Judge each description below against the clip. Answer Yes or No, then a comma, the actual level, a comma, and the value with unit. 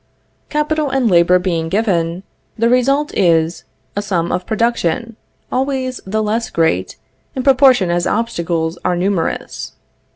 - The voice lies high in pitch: Yes, high, 205 Hz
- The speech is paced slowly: Yes, slow, 130 wpm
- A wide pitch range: Yes, wide, 6.6 semitones